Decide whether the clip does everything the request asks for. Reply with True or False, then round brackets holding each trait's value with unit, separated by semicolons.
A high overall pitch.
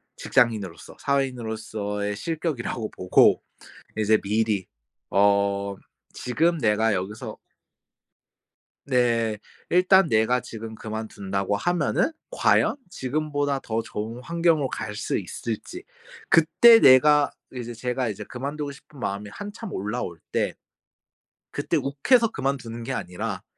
False (115 Hz)